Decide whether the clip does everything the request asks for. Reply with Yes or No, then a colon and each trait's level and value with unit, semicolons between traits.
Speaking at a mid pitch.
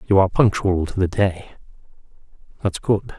No: very low, 95 Hz